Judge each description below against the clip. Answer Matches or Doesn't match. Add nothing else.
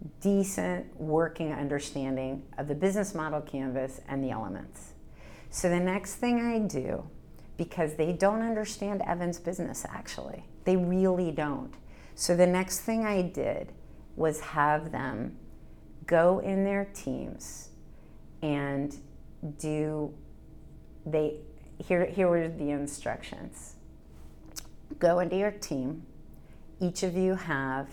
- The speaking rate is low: Matches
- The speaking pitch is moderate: Matches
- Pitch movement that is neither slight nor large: Matches